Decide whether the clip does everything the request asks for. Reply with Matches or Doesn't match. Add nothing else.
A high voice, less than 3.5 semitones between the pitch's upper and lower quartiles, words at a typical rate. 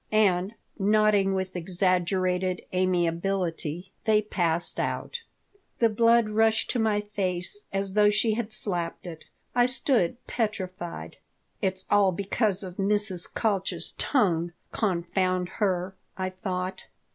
Doesn't match